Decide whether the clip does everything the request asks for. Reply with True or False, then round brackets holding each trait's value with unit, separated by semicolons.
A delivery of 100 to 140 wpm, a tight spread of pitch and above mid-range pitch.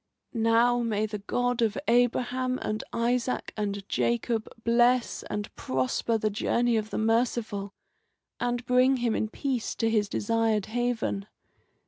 True (135 wpm; 2.3 semitones; 230 Hz)